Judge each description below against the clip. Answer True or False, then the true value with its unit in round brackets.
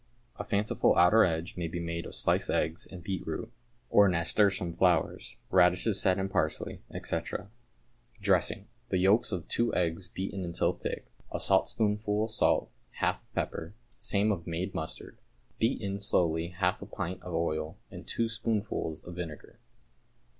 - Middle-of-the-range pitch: False (90 Hz)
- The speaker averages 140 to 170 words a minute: True (155 wpm)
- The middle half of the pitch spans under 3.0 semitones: False (3.3 semitones)